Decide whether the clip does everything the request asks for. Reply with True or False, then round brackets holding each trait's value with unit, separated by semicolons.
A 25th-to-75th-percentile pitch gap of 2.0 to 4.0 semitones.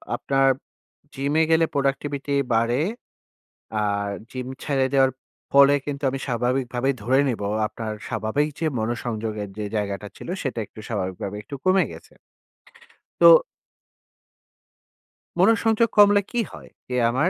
False (4.4 semitones)